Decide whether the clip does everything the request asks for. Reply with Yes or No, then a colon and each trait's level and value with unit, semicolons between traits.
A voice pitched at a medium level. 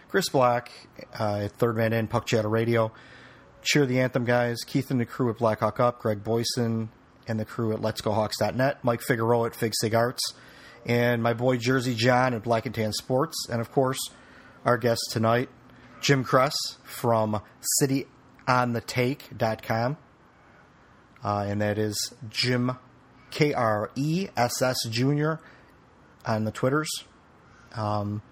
No: low, 120 Hz